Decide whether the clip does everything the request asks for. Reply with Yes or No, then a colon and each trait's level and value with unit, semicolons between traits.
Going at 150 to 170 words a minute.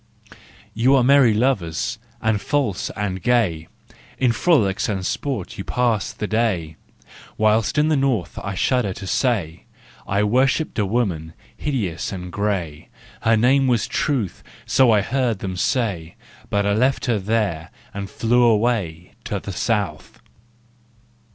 Yes: average, 165 wpm